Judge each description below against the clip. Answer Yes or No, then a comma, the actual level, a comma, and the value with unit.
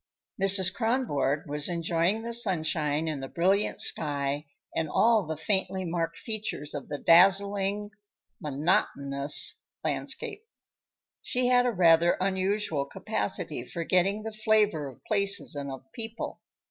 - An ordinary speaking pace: No, slow, 130 wpm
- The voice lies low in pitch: No, medium, 180 Hz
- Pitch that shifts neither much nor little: No, wide, 5.8 semitones